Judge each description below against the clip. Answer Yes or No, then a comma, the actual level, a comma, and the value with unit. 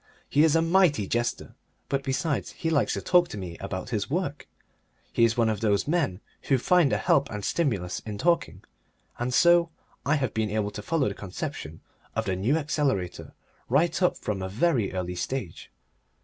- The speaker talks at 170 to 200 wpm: Yes, average, 190 wpm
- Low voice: Yes, low, 125 Hz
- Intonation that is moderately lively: No, wide, 7.7 semitones